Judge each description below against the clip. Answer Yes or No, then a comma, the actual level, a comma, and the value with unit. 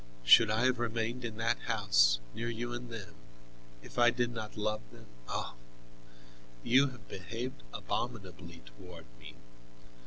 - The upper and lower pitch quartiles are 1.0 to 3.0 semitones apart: Yes, narrow, 2.5 semitones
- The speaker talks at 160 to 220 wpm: No, average, 145 wpm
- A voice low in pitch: Yes, low, 115 Hz